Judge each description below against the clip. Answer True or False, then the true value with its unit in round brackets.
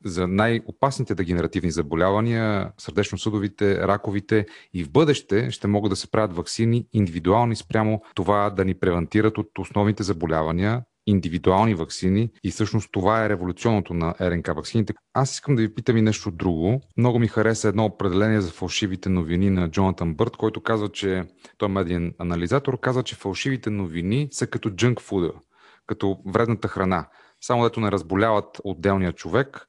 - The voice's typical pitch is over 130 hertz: False (105 Hz)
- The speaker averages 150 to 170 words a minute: True (160 wpm)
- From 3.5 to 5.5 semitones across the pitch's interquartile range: False (3.0 semitones)